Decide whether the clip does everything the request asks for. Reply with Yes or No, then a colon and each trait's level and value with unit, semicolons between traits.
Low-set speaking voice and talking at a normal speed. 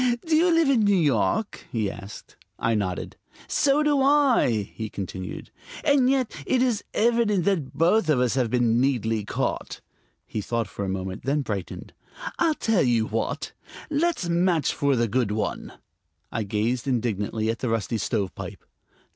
Yes: low, 130 Hz; average, 165 wpm